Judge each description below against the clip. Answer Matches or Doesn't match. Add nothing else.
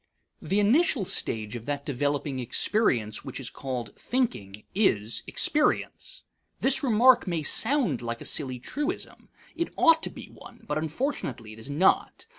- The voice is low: Doesn't match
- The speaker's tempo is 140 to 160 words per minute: Matches